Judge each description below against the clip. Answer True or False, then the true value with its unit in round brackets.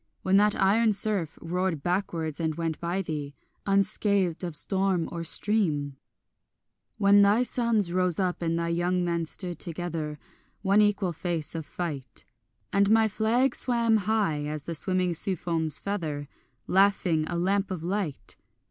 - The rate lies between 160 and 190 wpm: False (150 wpm)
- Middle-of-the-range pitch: True (180 Hz)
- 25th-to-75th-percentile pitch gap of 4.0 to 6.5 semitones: False (3.6 semitones)